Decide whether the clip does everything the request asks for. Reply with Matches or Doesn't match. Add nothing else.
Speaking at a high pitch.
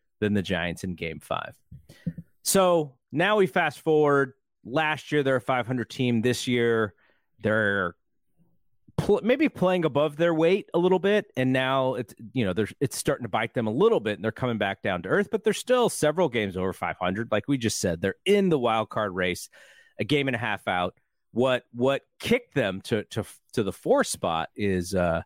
Doesn't match